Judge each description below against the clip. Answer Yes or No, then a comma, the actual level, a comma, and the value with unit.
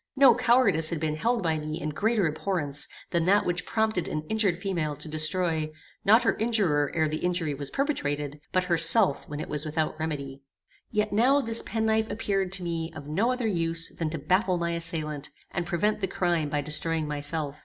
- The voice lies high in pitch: No, medium, 170 Hz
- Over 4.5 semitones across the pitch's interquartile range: Yes, average, 5.2 semitones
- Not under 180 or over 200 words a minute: Yes, average, 195 wpm